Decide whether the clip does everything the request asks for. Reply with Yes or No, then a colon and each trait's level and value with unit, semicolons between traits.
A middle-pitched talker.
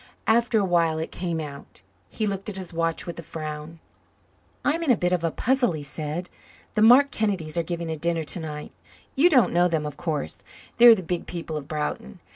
Yes: medium, 170 Hz